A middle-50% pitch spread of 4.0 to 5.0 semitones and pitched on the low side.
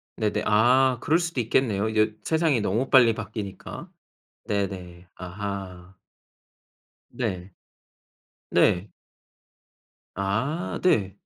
Yes: average, 4.6 semitones; low, 105 Hz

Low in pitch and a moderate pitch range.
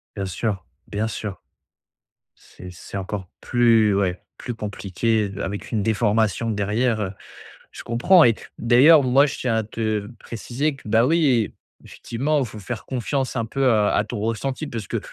Yes: low, 110 Hz; average, 3.2 semitones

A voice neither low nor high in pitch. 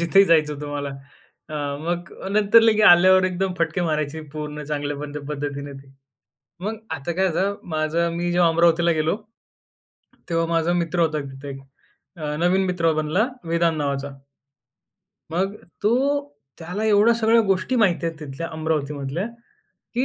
Yes: medium, 165 Hz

